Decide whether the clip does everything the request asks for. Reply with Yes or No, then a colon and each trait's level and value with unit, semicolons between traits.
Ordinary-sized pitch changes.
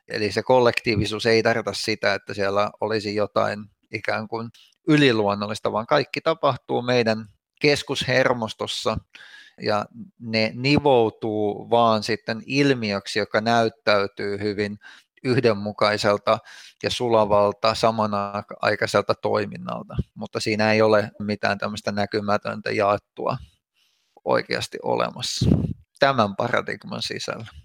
No: narrow, 2.2 semitones